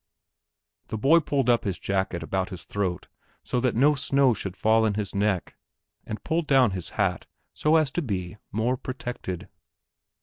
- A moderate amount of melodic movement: No, wide, 5.9 semitones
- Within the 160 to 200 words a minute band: Yes, average, 170 wpm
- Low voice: Yes, low, 110 Hz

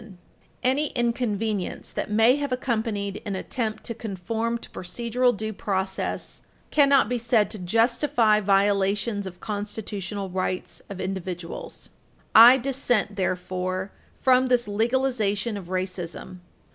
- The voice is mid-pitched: No, high, 215 Hz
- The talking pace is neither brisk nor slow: No, slow, 125 wpm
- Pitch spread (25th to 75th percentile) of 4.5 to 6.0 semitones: No, average, 3.8 semitones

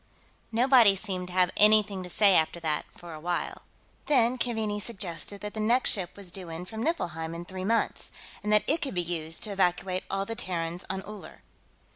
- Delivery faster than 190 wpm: Yes, average, 200 wpm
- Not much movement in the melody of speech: No, average, 3.7 semitones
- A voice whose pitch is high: Yes, high, 195 Hz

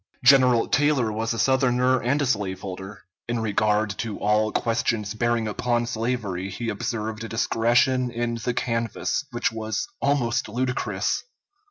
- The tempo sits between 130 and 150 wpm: Yes, average, 140 wpm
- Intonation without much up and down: Yes, narrow, 2.3 semitones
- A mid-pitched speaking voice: No, low, 115 Hz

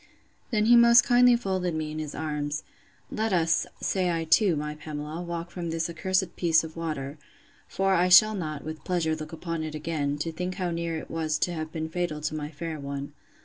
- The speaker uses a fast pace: Yes, fast, 210 wpm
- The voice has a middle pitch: Yes, medium, 165 Hz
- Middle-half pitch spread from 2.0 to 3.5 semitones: Yes, average, 2.7 semitones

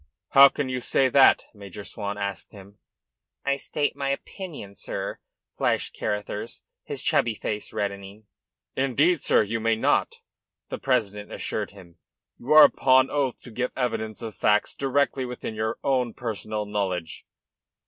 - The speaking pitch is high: No, low, 115 Hz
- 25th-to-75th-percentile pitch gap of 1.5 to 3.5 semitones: No, average, 4.5 semitones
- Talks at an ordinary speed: Yes, average, 150 wpm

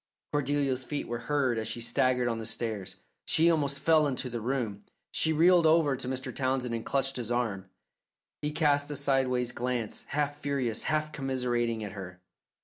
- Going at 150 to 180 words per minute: Yes, average, 175 wpm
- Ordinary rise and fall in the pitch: Yes, average, 3.4 semitones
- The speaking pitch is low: Yes, low, 130 Hz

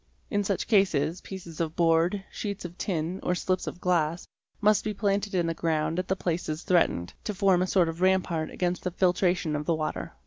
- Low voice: No, medium, 180 Hz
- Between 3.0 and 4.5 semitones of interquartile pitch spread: No, narrow, 2.6 semitones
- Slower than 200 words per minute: No, fast, 205 wpm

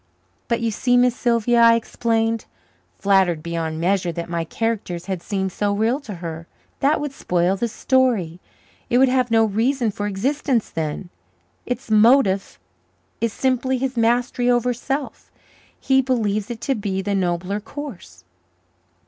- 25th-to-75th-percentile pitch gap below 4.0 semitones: No, average, 4.6 semitones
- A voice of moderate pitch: No, high, 225 Hz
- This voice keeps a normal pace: Yes, average, 150 wpm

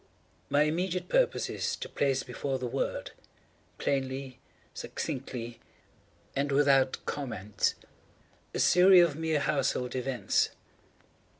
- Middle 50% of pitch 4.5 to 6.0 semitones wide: No, average, 2.9 semitones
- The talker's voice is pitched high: No, medium, 140 Hz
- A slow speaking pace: Yes, slow, 105 wpm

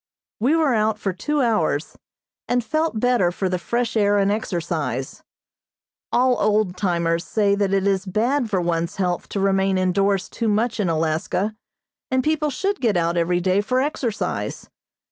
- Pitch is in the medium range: No, high, 200 Hz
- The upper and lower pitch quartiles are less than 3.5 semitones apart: No, average, 4.9 semitones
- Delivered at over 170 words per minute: No, average, 165 wpm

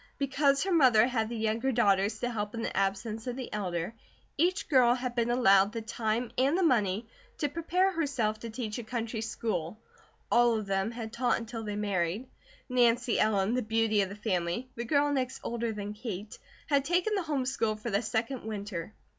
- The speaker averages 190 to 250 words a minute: Yes, average, 195 wpm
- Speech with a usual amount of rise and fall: Yes, average, 3.3 semitones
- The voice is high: Yes, high, 230 Hz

